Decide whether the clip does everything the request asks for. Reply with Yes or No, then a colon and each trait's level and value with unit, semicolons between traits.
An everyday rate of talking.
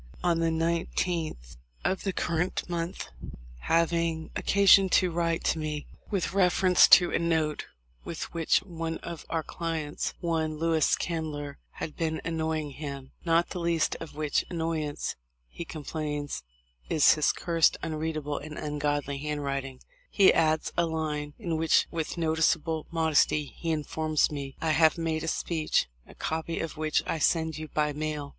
Yes: average, 150 wpm